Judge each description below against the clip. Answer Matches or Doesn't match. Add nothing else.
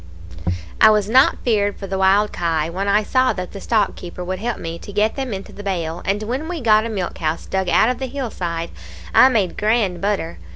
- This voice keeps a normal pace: Doesn't match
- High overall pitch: Matches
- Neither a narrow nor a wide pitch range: Matches